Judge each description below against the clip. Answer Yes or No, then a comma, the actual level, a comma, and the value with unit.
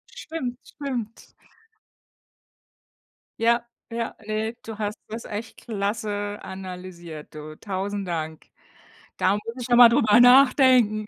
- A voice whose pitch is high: Yes, high, 215 Hz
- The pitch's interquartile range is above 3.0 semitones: Yes, average, 3.5 semitones